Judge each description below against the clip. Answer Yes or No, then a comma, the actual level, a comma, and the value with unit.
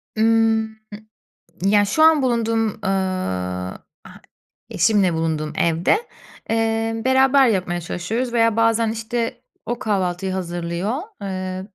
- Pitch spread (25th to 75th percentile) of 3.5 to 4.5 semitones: Yes, average, 3.8 semitones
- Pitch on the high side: Yes, high, 215 Hz